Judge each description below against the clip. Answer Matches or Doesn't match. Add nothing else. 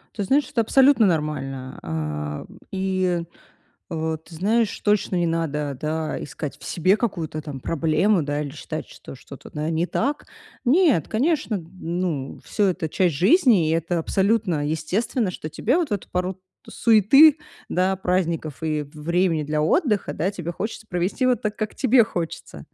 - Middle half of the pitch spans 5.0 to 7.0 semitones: Matches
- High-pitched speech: Doesn't match